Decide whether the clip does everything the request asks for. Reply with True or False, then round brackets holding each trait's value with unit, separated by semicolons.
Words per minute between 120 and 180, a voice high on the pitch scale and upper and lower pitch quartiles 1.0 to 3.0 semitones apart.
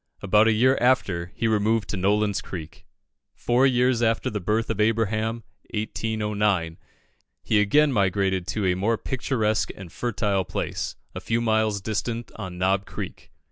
False (150 wpm; 105 Hz; 2.7 semitones)